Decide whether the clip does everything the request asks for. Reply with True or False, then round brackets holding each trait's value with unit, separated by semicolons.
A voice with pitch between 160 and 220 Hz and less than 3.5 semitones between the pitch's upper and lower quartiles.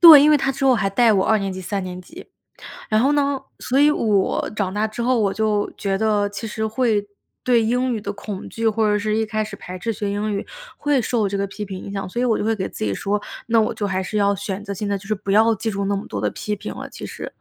True (210 Hz; 2.4 semitones)